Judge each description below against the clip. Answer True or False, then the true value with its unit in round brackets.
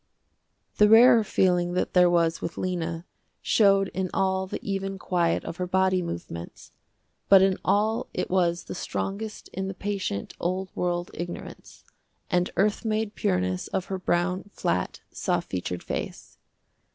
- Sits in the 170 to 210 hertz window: True (185 Hz)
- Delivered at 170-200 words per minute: False (150 wpm)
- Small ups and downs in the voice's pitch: True (2.1 semitones)